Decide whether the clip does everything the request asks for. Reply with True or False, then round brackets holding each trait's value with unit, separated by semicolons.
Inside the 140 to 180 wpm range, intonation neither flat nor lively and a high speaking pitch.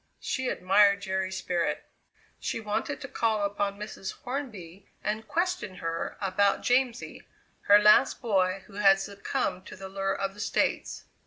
False (150 wpm; 2.2 semitones; 200 Hz)